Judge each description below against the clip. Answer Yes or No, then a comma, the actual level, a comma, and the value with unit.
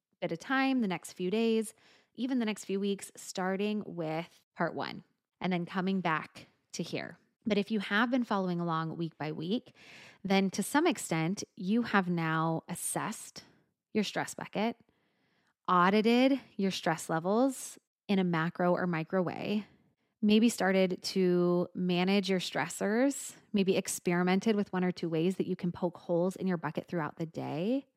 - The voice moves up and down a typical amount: Yes, average, 3.5 semitones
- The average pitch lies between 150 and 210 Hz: Yes, high, 190 Hz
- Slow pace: No, average, 165 wpm